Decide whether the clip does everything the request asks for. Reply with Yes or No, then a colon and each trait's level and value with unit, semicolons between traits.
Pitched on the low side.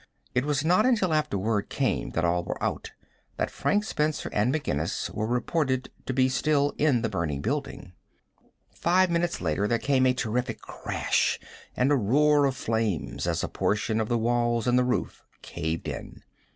Yes: low, 125 Hz